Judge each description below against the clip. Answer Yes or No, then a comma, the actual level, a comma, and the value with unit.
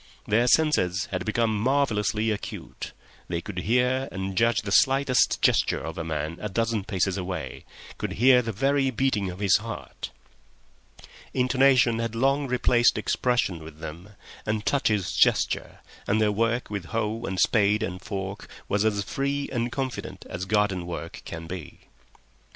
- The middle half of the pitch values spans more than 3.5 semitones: Yes, average, 4.6 semitones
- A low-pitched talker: Yes, low, 110 Hz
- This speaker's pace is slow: No, average, 150 wpm